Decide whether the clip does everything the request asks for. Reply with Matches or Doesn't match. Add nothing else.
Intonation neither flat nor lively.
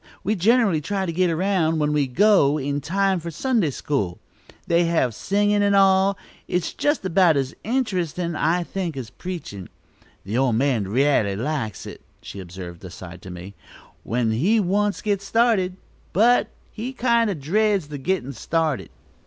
Doesn't match